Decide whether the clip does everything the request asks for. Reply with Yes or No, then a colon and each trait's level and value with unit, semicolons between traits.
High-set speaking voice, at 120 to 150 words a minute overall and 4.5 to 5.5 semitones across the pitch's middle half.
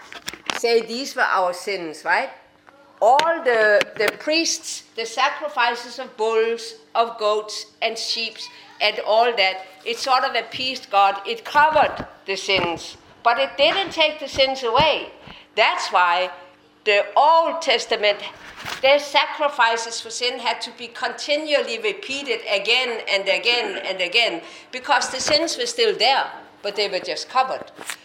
Yes: high, 235 Hz; average, 145 wpm; average, 5.2 semitones